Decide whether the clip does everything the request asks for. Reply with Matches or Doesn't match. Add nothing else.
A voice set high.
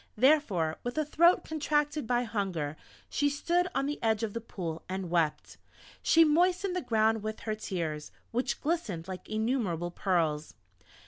Matches